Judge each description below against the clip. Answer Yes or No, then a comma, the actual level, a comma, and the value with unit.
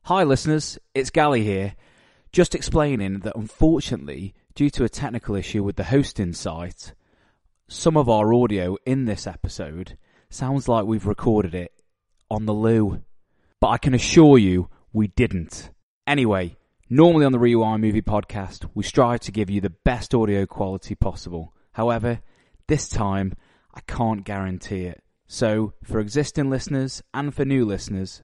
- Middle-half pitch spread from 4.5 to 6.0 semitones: Yes, average, 4.9 semitones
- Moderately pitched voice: No, low, 110 Hz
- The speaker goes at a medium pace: Yes, average, 155 wpm